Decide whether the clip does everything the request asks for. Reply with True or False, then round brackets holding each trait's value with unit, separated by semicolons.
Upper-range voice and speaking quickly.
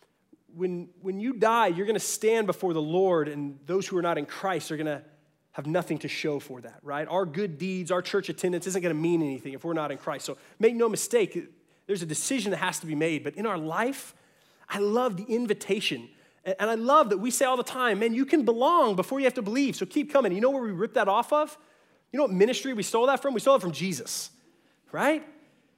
True (195 Hz; 240 wpm)